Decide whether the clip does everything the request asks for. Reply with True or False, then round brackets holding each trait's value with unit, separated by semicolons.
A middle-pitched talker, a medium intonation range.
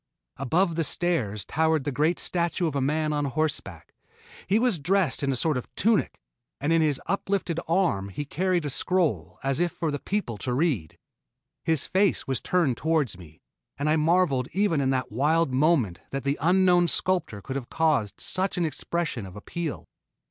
True (155 Hz; 4.7 semitones)